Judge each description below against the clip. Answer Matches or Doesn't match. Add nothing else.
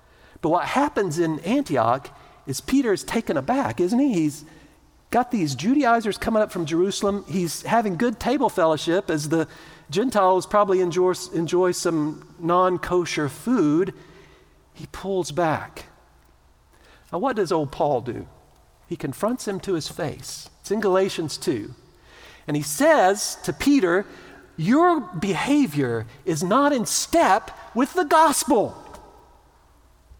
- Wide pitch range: Matches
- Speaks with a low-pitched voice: Doesn't match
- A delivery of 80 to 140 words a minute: Matches